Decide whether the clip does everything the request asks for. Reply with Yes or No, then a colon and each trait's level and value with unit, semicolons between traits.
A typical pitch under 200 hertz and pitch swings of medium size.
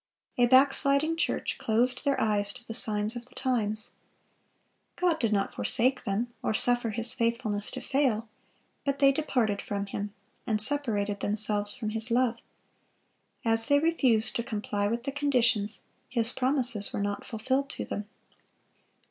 No: high, 235 Hz; average, 3.7 semitones